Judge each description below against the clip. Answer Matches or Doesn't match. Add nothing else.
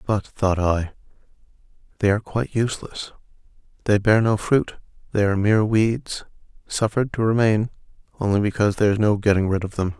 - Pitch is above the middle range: Doesn't match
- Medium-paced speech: Matches